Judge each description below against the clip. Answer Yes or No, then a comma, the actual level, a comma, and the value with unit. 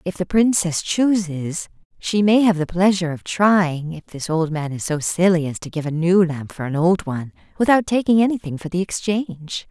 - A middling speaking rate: No, fast, 210 wpm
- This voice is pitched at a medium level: Yes, medium, 175 Hz